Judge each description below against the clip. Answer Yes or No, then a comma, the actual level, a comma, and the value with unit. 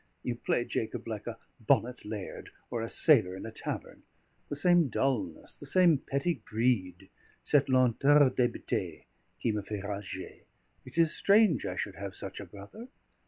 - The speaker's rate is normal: Yes, average, 165 wpm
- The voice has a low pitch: Yes, low, 120 Hz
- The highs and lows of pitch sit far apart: Yes, wide, 5.9 semitones